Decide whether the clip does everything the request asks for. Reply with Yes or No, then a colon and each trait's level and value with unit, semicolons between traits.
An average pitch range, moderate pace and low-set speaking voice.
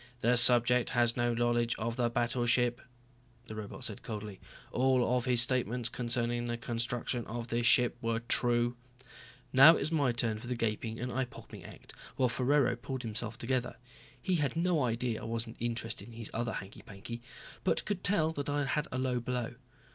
No: narrow, 1.4 semitones; average, 185 wpm; low, 120 Hz